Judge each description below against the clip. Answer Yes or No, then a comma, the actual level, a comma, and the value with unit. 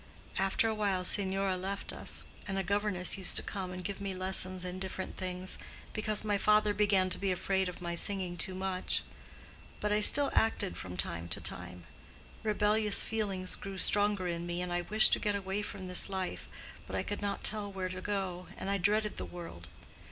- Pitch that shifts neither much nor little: No, narrow, 2.1 semitones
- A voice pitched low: No, high, 190 Hz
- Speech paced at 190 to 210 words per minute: Yes, average, 200 wpm